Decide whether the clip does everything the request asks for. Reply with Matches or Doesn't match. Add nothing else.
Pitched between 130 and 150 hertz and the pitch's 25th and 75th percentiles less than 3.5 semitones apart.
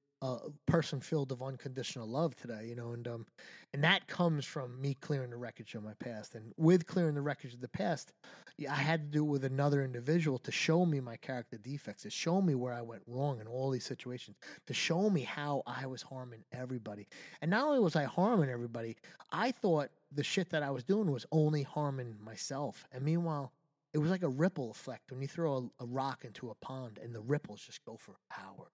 Doesn't match